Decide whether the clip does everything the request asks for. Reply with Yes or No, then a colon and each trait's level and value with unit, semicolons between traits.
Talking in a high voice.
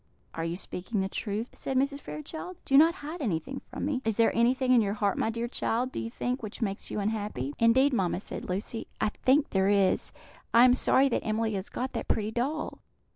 Yes: high, 230 Hz